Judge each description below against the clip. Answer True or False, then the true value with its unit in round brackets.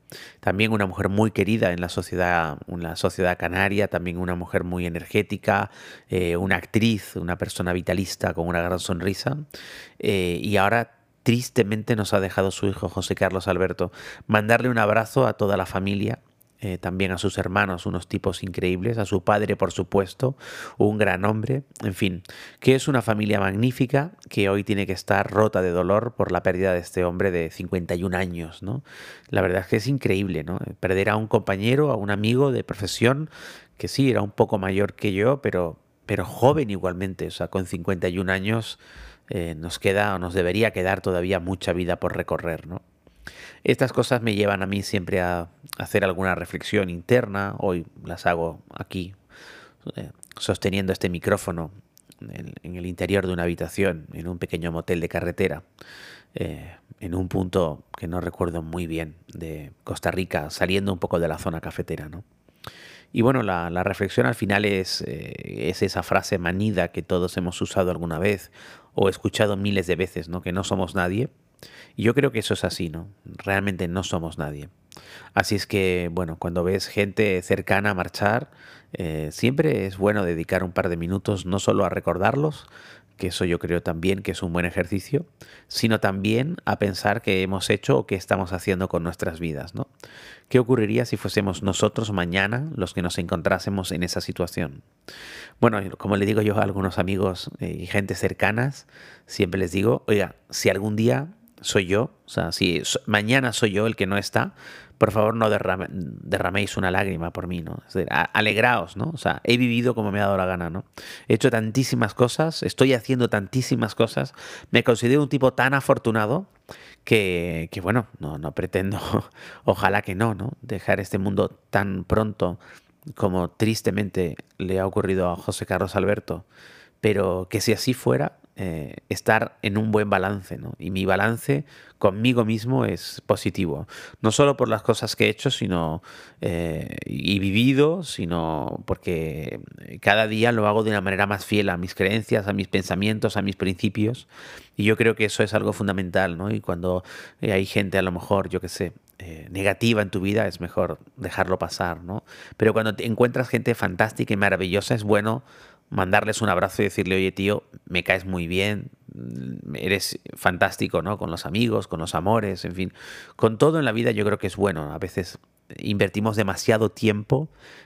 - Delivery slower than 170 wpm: False (180 wpm)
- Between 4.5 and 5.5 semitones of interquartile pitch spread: False (3.3 semitones)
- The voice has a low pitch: True (100 Hz)